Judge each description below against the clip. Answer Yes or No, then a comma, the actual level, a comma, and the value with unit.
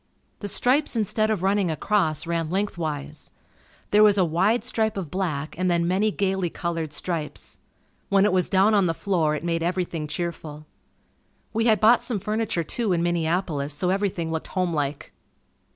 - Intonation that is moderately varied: Yes, average, 3.9 semitones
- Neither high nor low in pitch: Yes, medium, 180 Hz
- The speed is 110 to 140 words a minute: No, average, 170 wpm